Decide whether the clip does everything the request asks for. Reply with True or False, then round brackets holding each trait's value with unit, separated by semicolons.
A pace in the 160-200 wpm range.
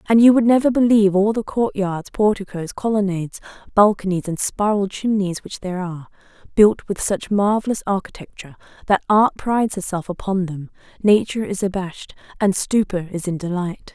False (150 wpm)